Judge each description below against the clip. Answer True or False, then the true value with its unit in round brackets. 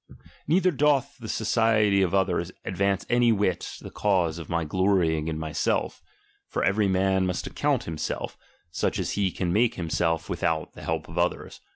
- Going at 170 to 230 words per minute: True (180 wpm)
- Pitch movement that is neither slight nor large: True (4.3 semitones)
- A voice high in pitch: False (95 Hz)